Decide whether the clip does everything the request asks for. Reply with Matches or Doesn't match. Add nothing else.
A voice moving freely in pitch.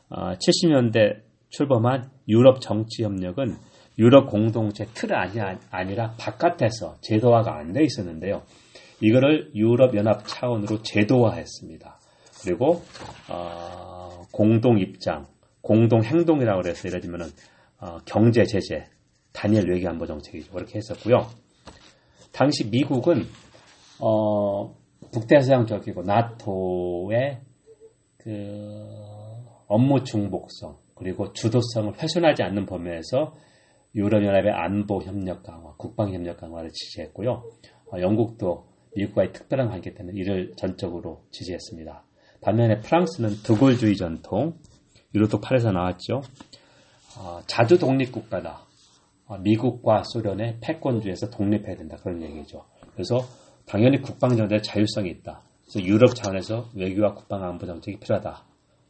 Doesn't match